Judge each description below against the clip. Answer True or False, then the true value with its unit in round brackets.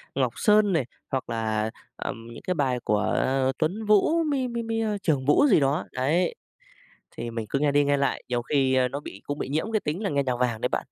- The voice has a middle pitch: True (145 Hz)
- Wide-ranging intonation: True (8.0 semitones)